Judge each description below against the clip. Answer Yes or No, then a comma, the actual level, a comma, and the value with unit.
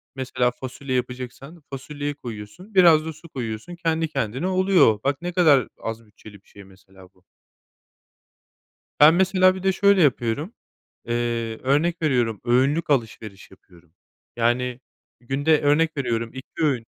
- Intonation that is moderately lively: No, wide, 5.8 semitones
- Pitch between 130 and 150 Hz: Yes, low, 135 Hz